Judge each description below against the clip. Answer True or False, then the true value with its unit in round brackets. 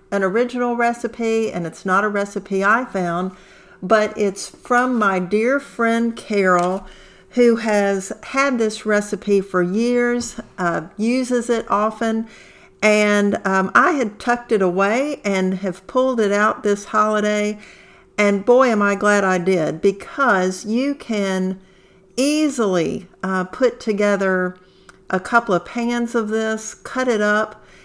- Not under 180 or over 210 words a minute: False (140 wpm)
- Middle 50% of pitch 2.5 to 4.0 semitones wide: True (3.6 semitones)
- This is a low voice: False (210 Hz)